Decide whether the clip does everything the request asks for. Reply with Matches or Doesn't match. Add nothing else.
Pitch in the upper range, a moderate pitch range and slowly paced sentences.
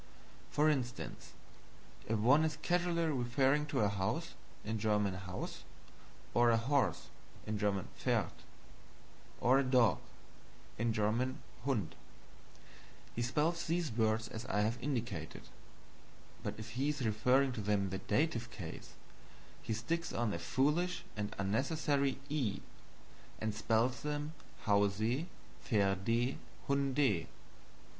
Doesn't match